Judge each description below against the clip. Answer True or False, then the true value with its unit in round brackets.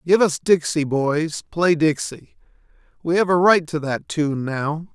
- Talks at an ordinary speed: True (170 wpm)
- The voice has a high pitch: False (160 Hz)